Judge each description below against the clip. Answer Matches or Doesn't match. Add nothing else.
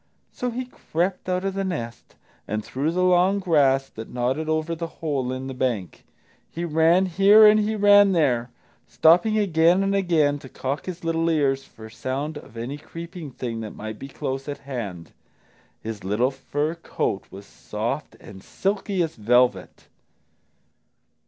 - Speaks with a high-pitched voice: Doesn't match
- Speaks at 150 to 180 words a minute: Matches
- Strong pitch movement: Matches